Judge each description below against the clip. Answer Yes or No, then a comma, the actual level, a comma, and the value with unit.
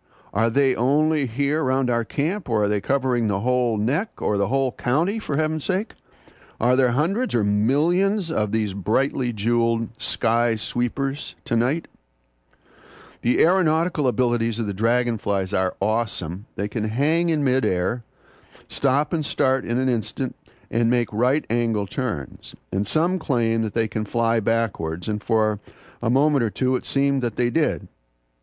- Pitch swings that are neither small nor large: Yes, average, 4.1 semitones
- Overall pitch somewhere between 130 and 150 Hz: No, low, 120 Hz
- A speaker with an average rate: Yes, average, 160 wpm